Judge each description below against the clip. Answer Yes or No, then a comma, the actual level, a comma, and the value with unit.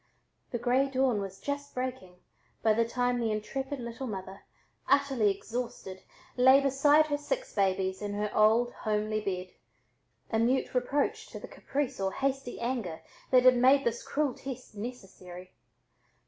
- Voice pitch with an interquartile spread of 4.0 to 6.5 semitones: Yes, average, 4.3 semitones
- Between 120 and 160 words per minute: Yes, average, 150 wpm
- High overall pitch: Yes, high, 245 Hz